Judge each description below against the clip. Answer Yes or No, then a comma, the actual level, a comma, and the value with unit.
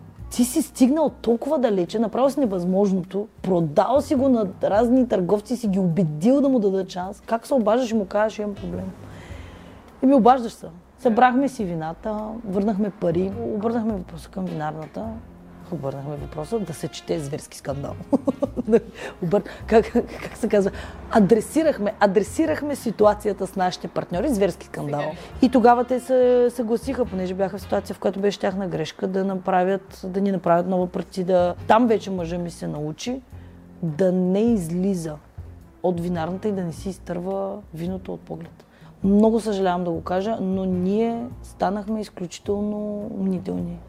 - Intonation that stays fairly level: No, average, 4.4 semitones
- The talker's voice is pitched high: Yes, high, 200 Hz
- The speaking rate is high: No, average, 155 wpm